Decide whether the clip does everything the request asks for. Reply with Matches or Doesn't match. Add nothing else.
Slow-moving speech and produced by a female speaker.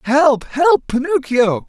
Doesn't match